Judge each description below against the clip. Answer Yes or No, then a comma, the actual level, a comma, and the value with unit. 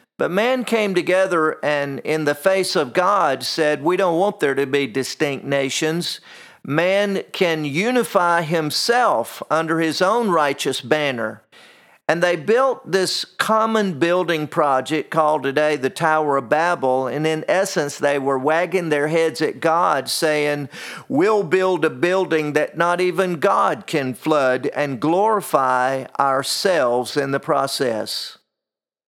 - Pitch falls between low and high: Yes, medium, 155 Hz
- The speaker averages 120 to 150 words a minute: Yes, average, 140 wpm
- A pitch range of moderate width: Yes, average, 4.3 semitones